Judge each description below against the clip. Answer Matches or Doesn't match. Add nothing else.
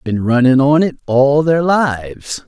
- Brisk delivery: Doesn't match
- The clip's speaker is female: Doesn't match